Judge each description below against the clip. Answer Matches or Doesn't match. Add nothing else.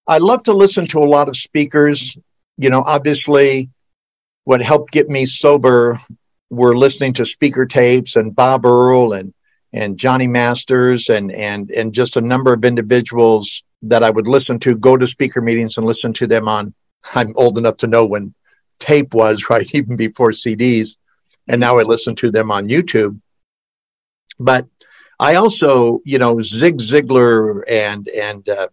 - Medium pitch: Doesn't match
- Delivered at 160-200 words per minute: Matches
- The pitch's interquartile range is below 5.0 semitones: Matches